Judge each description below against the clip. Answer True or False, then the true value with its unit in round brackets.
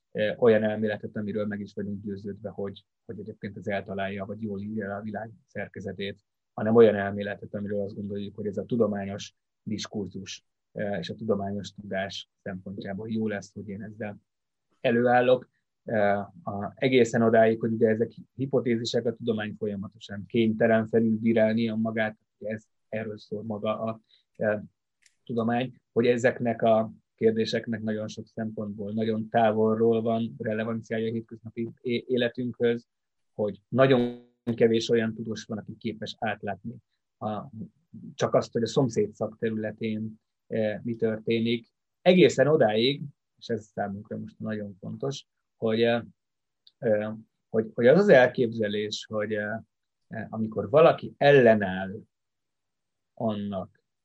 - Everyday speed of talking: True (130 wpm)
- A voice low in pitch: True (110 Hz)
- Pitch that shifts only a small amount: True (2.0 semitones)